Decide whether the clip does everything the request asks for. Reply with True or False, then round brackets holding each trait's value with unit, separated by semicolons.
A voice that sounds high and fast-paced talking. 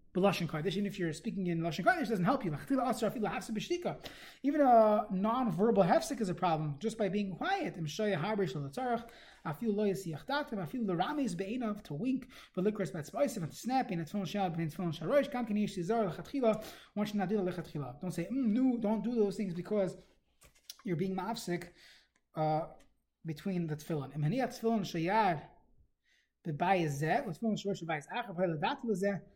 True (200 Hz; 210 wpm)